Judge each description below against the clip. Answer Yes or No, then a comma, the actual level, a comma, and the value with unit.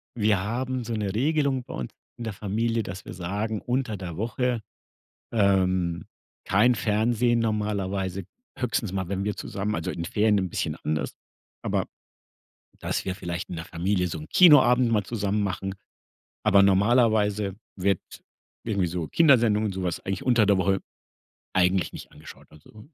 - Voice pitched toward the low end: Yes, low, 105 Hz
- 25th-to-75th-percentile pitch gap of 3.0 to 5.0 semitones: Yes, average, 3.5 semitones